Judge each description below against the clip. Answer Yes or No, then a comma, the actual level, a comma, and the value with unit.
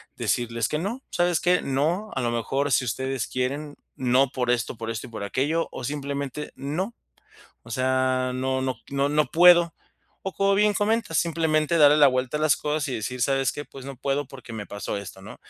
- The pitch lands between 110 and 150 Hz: Yes, medium, 140 Hz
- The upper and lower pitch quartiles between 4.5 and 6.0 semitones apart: No, average, 3.5 semitones